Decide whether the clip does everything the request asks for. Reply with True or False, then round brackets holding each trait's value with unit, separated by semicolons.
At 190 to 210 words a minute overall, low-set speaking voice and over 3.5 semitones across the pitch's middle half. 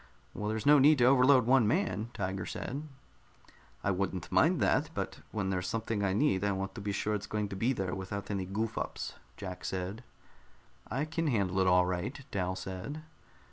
True (195 wpm; 100 Hz; 4.7 semitones)